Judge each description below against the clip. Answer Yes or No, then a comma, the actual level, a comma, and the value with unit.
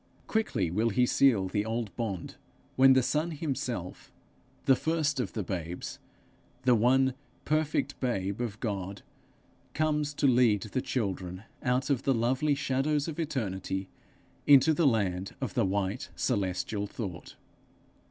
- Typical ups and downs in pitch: No, wide, 5.8 semitones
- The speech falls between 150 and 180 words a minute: No, average, 140 wpm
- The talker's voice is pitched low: Yes, low, 120 Hz